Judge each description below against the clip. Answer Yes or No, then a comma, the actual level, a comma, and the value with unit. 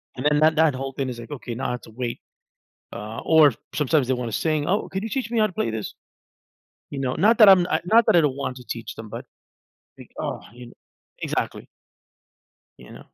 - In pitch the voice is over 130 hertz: Yes, medium, 140 Hz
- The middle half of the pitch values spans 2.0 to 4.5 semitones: No, average, 5.2 semitones